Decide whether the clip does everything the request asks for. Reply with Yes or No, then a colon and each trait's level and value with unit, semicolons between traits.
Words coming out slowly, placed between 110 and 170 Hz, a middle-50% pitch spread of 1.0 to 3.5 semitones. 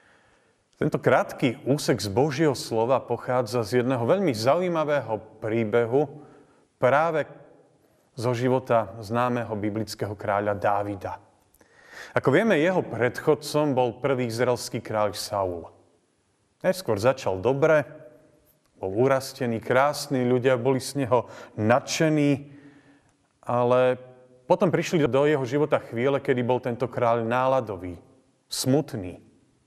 No: slow, 105 wpm; low, 125 Hz; average, 4.0 semitones